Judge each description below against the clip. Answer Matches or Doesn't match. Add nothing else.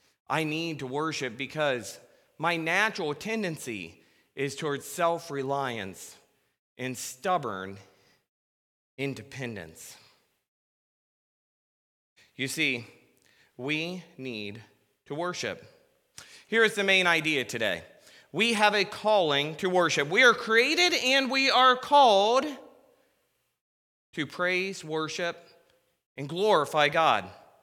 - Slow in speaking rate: Matches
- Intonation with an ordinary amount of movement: Doesn't match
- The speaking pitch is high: Doesn't match